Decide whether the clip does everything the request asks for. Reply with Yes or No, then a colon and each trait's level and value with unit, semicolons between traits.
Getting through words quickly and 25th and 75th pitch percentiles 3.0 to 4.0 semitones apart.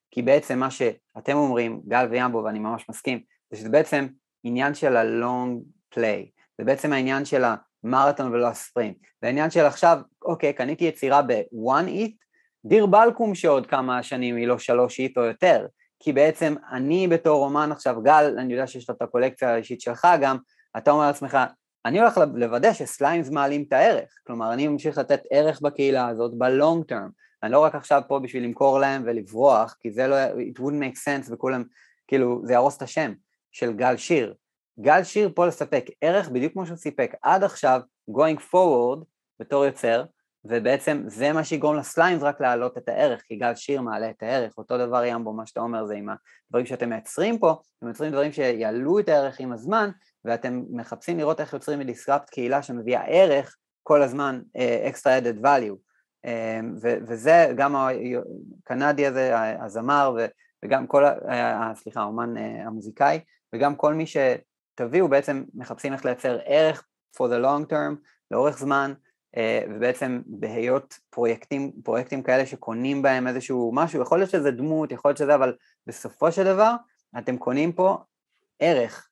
Yes: fast, 170 wpm; average, 3.7 semitones